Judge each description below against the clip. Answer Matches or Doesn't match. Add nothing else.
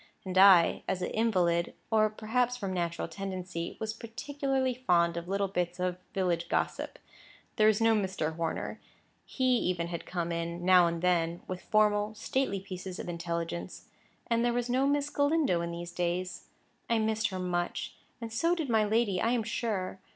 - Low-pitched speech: Doesn't match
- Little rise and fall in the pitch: Doesn't match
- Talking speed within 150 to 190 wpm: Matches